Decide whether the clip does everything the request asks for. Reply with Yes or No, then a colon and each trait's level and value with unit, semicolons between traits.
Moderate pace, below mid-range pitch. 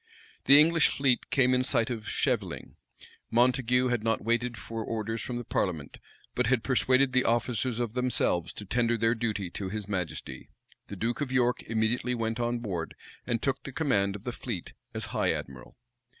Yes: average, 180 wpm; low, 120 Hz